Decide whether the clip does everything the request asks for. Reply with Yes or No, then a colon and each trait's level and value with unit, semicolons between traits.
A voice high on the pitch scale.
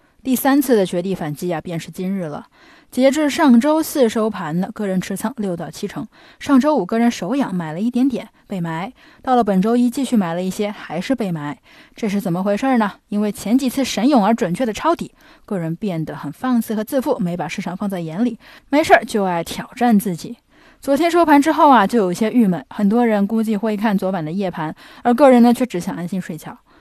Yes: high, 220 Hz